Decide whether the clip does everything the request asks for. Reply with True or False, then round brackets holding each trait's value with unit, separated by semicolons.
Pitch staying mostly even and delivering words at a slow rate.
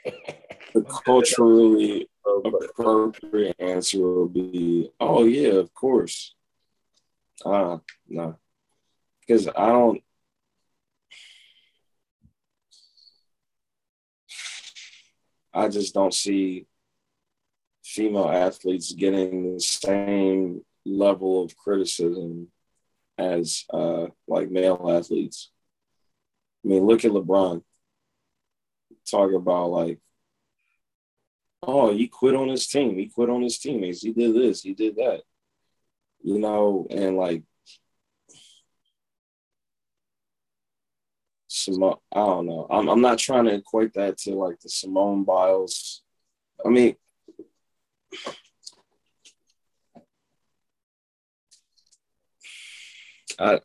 False (3.8 semitones; 90 wpm)